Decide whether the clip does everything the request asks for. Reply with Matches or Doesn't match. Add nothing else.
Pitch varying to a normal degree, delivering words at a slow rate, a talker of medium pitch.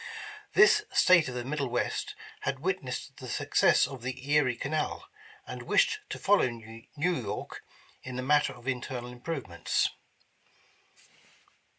Doesn't match